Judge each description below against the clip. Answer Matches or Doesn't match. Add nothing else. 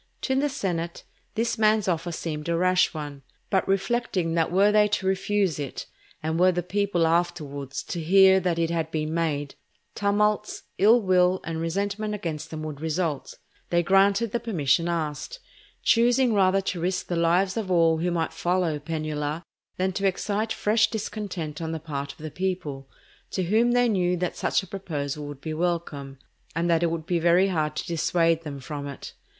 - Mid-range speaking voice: Matches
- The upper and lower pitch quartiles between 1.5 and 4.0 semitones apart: Matches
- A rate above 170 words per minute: Matches